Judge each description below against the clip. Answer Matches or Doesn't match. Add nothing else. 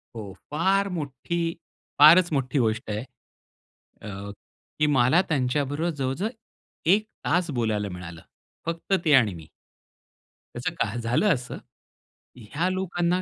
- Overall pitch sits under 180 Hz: Matches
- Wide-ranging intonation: Matches